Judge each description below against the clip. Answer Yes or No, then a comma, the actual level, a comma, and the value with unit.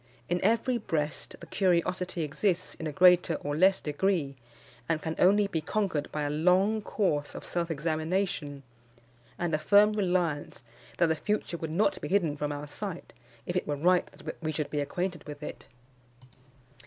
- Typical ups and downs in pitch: Yes, average, 3.9 semitones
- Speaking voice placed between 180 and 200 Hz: No, medium, 170 Hz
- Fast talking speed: No, average, 175 wpm